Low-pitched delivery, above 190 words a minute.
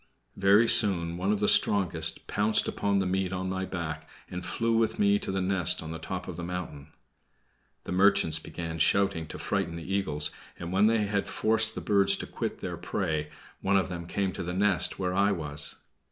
Yes: very low, 95 Hz; fast, 205 wpm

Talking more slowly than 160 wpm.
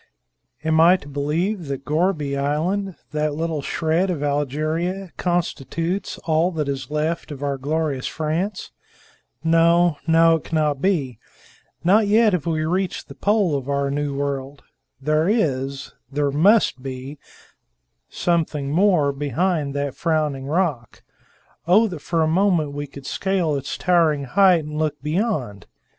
Yes: average, 145 wpm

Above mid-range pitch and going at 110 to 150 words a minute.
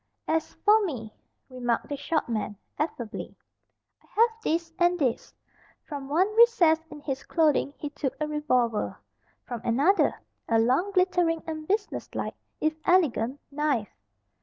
Yes: very high, 300 Hz; average, 140 wpm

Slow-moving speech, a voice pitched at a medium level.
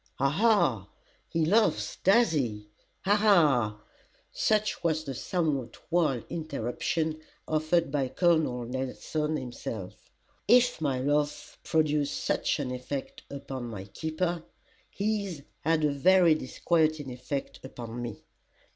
Yes: slow, 120 wpm; medium, 150 Hz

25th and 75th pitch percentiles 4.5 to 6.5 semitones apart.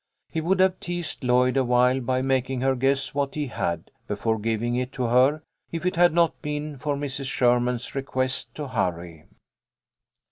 No: average, 3.1 semitones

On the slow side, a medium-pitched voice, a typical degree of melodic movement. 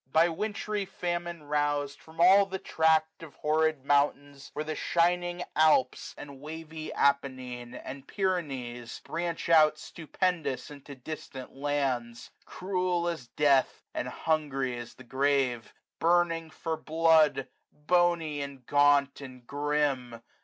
Yes: slow, 125 wpm; medium, 150 Hz; average, 3.3 semitones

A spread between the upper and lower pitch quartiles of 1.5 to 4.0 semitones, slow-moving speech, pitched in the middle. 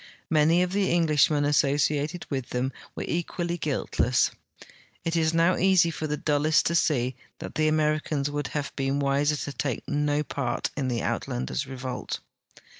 No: average, 2.7 semitones; average, 165 wpm; medium, 150 Hz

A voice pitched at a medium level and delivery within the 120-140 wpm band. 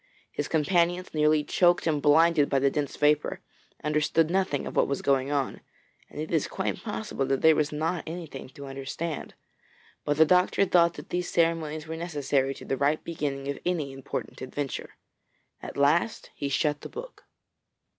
No: medium, 150 Hz; average, 175 wpm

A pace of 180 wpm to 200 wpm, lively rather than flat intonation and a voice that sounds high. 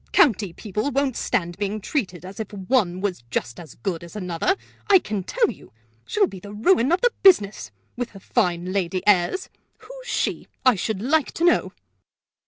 Yes: average, 185 wpm; wide, 7.5 semitones; high, 210 Hz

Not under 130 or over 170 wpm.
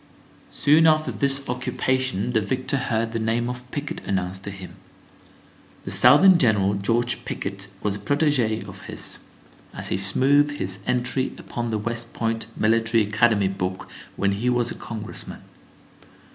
Yes: average, 150 wpm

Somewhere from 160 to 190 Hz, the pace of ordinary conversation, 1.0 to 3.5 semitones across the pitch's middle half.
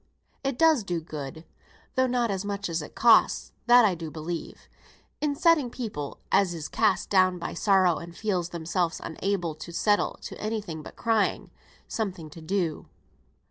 No: medium, 185 Hz; average, 170 wpm; average, 4.8 semitones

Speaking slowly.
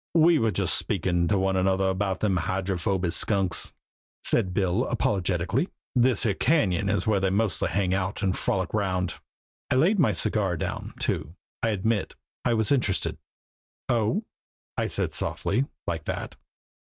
No: average, 155 wpm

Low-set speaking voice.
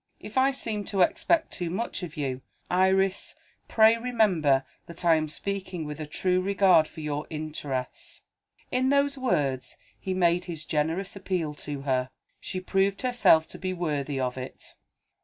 No: medium, 180 Hz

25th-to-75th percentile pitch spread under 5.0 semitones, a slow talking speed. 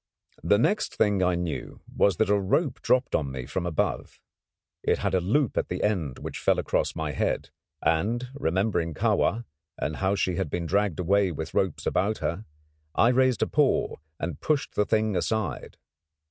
No: average, 4.4 semitones; average, 180 wpm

